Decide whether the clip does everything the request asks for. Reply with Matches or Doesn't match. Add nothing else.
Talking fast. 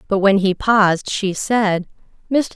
Doesn't match